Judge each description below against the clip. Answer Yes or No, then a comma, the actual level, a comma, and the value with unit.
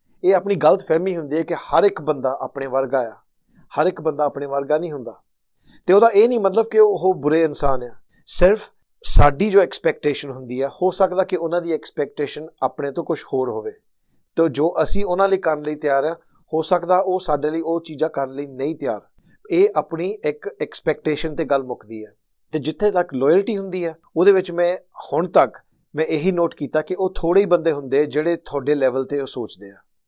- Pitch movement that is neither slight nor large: Yes, average, 4.5 semitones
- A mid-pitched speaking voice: Yes, medium, 160 Hz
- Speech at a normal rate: No, fast, 205 wpm